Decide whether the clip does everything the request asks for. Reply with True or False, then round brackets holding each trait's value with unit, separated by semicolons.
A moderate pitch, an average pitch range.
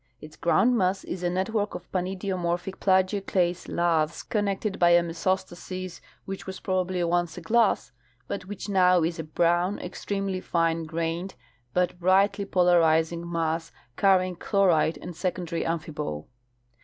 False (180 Hz; 2.2 semitones)